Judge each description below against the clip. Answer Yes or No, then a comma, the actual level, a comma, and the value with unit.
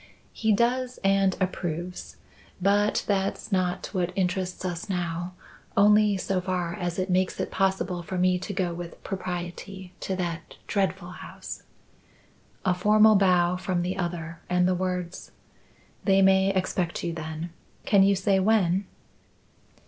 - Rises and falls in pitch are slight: Yes, narrow, 1.7 semitones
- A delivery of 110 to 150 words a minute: Yes, average, 140 wpm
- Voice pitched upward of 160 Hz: Yes, medium, 185 Hz